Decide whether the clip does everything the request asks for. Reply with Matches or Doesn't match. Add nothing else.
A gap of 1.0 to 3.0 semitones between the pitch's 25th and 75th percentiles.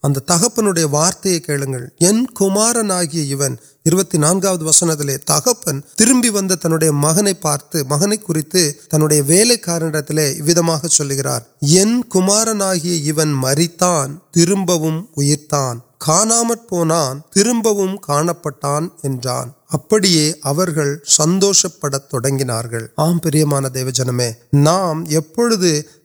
Doesn't match